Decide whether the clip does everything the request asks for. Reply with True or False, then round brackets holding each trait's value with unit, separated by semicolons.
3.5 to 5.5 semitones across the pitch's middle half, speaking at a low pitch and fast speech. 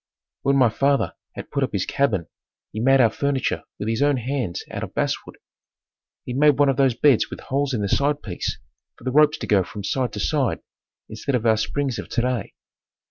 True (3.8 semitones; 130 Hz; 210 wpm)